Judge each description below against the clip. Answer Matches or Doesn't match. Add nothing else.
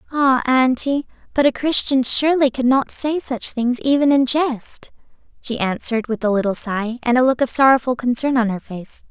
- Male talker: Doesn't match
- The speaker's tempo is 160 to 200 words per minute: Matches